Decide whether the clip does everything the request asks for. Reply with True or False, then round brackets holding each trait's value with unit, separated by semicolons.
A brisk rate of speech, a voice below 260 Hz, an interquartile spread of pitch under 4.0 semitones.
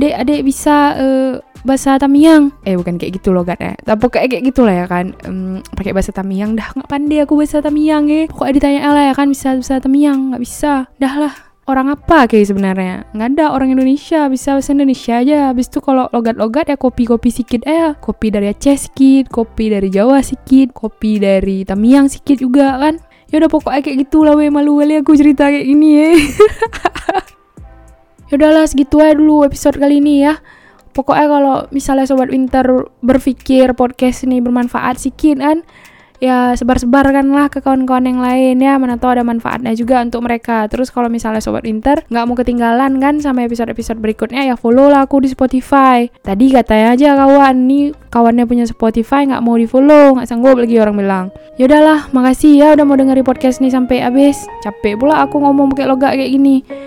False (190 wpm; 265 Hz; 2.9 semitones)